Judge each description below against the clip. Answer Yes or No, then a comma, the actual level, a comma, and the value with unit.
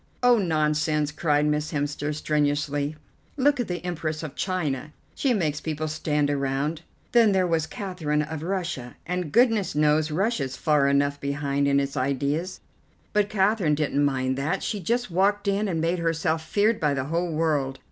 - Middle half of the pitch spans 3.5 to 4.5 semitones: Yes, average, 4.1 semitones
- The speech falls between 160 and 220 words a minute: Yes, average, 165 wpm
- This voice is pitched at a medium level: Yes, medium, 155 Hz